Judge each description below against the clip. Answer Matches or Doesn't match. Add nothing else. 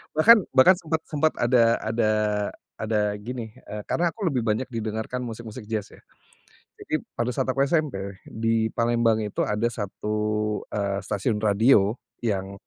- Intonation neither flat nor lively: Matches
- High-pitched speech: Doesn't match